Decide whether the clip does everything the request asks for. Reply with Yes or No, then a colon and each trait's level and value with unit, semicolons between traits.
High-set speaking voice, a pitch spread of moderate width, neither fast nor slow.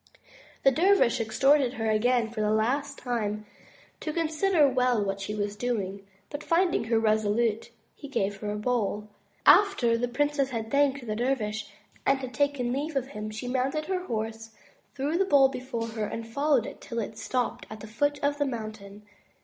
Yes: high, 245 Hz; average, 4.6 semitones; average, 180 wpm